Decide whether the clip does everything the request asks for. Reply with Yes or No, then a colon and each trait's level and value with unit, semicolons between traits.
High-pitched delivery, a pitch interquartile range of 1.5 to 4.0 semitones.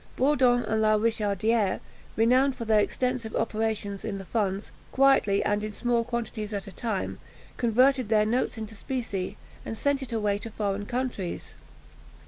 Yes: high, 220 Hz; average, 2.8 semitones